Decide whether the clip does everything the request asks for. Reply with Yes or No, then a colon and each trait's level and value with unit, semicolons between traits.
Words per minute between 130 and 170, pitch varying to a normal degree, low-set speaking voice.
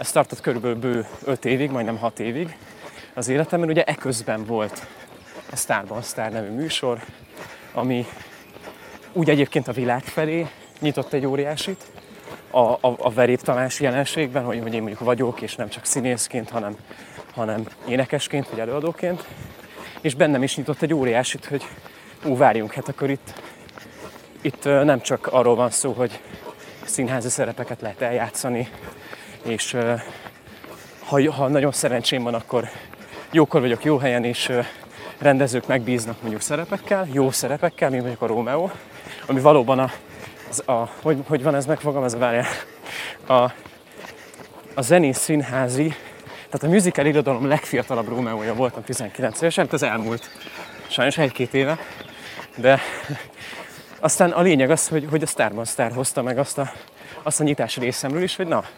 Yes: average, 150 wpm; average, 3.6 semitones; low, 130 Hz